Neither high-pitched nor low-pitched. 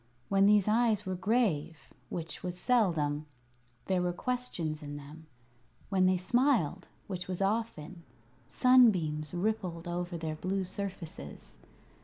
Yes: medium, 180 Hz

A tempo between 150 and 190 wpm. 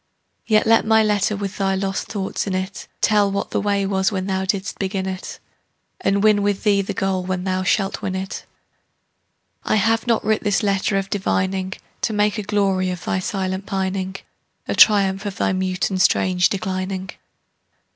Yes: average, 185 wpm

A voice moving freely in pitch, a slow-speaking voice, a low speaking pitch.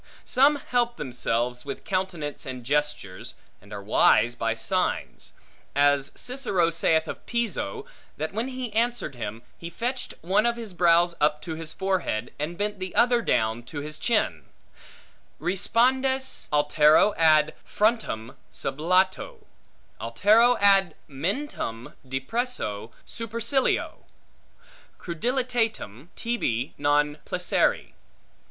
No: wide, 8.6 semitones; slow, 115 wpm; medium, 170 Hz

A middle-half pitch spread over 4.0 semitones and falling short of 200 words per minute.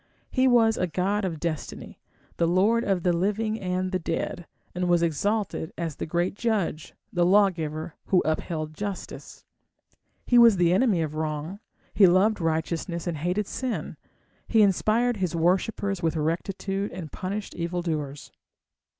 No: average, 3.7 semitones; average, 150 wpm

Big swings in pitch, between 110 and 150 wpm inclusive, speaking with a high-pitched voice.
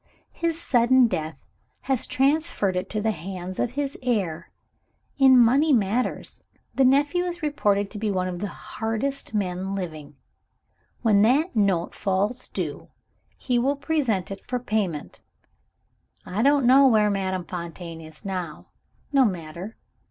Yes: wide, 6.1 semitones; average, 145 wpm; high, 215 Hz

